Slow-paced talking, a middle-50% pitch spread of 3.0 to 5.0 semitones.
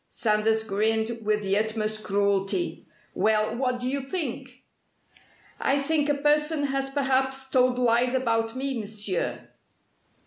Yes: slow, 130 wpm; average, 3.9 semitones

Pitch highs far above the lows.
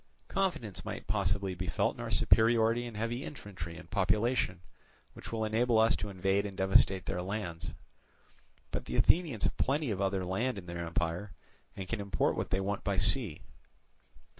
No: average, 3.7 semitones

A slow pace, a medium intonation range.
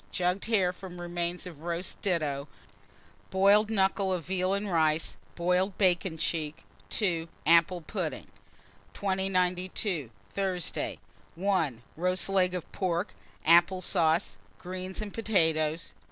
No: slow, 115 wpm; narrow, 2.2 semitones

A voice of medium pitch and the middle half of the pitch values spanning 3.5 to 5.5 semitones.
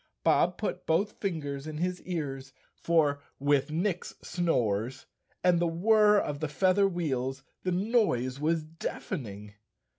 Yes: medium, 160 Hz; average, 5.1 semitones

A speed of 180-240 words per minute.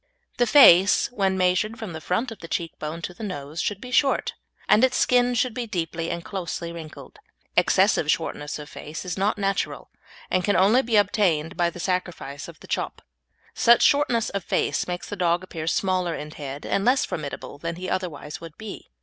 Yes: average, 200 wpm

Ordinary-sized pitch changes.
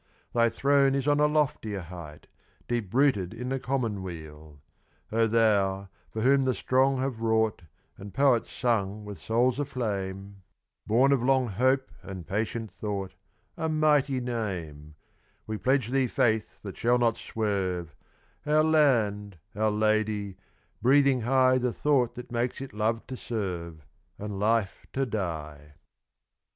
Yes: average, 4.8 semitones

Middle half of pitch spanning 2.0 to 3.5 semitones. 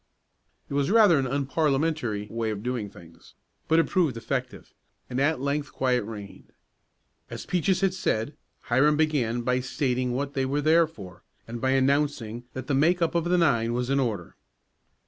No: average, 4.3 semitones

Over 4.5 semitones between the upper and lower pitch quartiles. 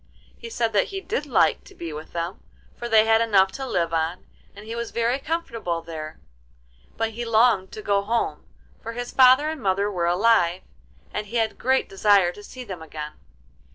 Yes: average, 4.9 semitones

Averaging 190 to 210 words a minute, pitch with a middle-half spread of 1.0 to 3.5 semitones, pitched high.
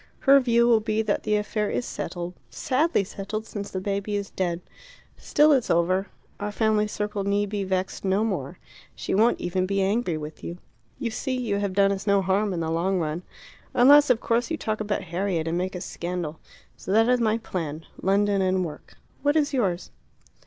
Yes: average, 200 wpm; average, 3.2 semitones; high, 200 Hz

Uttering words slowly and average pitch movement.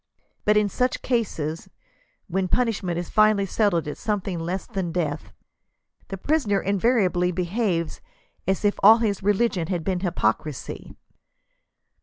Yes: slow, 130 wpm; average, 3.5 semitones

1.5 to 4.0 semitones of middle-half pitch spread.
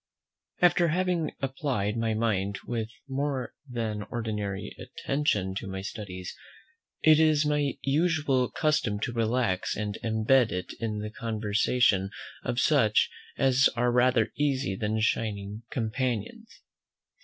No: average, 4.6 semitones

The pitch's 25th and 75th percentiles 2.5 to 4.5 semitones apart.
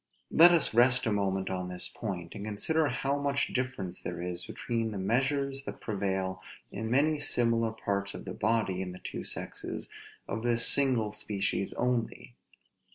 No: average, 5.0 semitones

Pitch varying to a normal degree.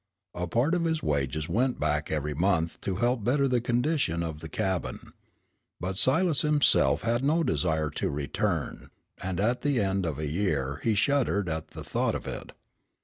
No: wide, 8.3 semitones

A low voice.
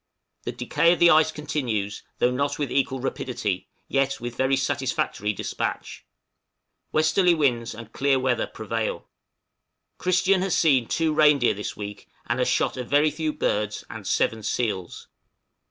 Yes: low, 130 Hz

